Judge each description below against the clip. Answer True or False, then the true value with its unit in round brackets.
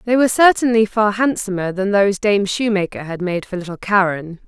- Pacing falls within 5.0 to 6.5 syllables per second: True (5.6 syllables/s)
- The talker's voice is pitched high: True (200 Hz)